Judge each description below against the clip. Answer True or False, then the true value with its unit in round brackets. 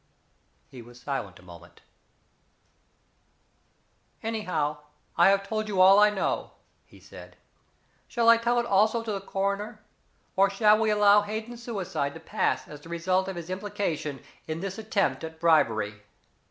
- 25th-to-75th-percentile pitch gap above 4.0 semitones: True (5.2 semitones)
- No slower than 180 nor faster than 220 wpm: False (155 wpm)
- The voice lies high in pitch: True (195 Hz)